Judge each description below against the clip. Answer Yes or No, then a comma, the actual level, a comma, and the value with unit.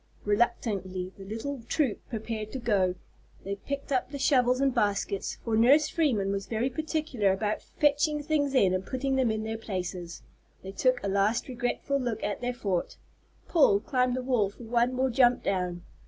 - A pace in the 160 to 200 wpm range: Yes, average, 180 wpm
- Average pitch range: Yes, average, 4.8 semitones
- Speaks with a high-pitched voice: Yes, high, 235 Hz